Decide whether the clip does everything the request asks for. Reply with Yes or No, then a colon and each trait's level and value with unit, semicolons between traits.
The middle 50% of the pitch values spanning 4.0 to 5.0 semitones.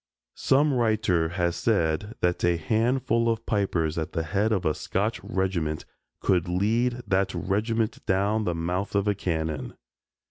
Yes: average, 4.4 semitones